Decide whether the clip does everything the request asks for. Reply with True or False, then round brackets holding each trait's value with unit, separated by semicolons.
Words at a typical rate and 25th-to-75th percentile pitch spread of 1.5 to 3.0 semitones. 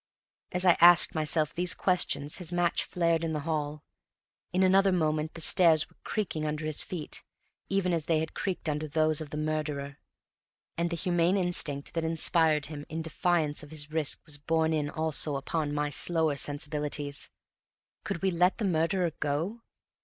True (175 wpm; 2.5 semitones)